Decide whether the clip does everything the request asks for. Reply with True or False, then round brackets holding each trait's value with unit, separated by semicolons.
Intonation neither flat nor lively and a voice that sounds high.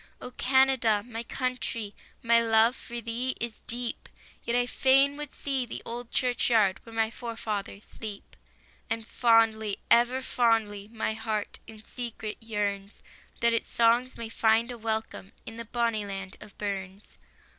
False (1.9 semitones; 230 Hz)